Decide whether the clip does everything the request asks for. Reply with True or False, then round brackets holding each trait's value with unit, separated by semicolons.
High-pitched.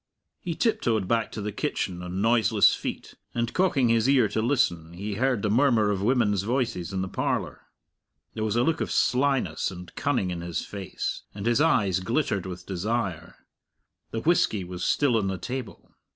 False (110 Hz)